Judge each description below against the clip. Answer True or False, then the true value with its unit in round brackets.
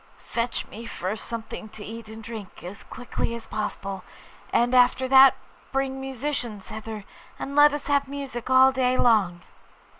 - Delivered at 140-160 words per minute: True (155 wpm)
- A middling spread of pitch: True (3.5 semitones)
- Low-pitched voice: False (235 Hz)